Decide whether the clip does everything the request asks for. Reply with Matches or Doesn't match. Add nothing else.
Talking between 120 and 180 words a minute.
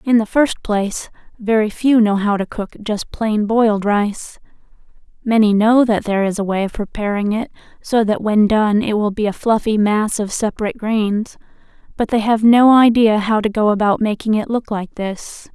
Doesn't match